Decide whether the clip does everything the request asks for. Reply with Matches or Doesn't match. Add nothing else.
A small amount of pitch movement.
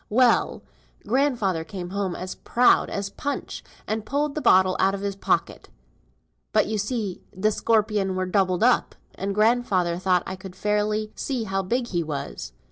Doesn't match